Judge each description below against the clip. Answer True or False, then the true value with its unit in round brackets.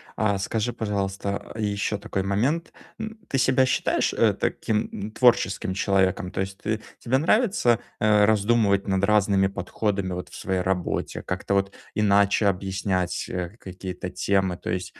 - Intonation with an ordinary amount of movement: False (2.2 semitones)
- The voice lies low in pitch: True (100 Hz)